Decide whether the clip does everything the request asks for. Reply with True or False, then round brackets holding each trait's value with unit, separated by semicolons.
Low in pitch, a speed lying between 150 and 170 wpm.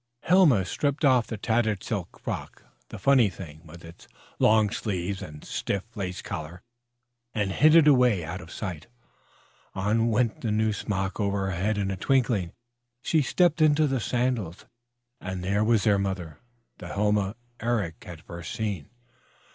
True (105 Hz; 160 wpm)